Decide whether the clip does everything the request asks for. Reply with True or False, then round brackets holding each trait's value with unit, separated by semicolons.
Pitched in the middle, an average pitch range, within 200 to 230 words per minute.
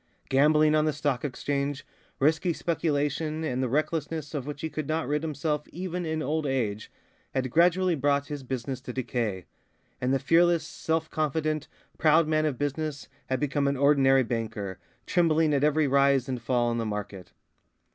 False (145 Hz; 3.0 semitones; 170 wpm)